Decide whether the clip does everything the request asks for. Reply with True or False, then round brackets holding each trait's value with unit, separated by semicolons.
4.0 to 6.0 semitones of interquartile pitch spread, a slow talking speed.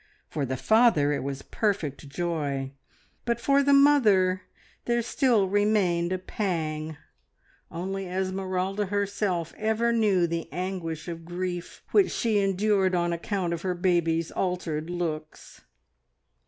False (3.6 semitones; 125 wpm)